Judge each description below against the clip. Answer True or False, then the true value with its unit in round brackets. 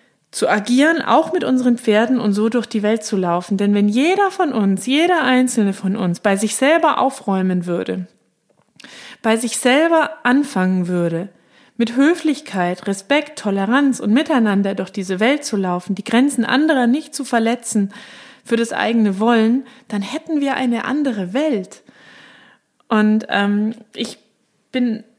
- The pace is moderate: True (150 wpm)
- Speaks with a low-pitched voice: False (230 Hz)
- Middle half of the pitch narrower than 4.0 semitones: False (4.8 semitones)